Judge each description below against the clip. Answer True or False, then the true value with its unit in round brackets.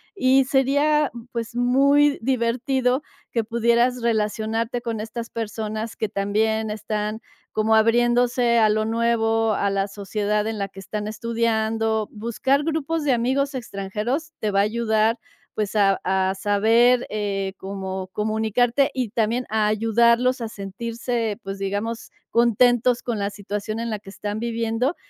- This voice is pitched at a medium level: False (225 Hz)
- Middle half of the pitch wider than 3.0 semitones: False (2.4 semitones)